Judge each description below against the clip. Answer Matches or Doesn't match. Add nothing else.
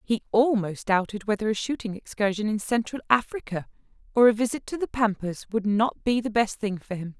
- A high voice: Matches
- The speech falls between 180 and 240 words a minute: Matches